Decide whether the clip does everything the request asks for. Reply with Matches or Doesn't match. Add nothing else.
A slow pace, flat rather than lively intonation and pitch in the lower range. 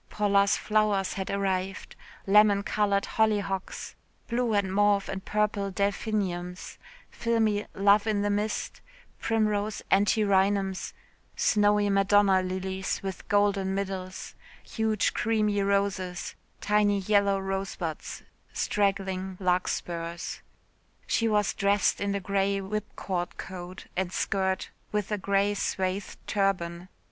Doesn't match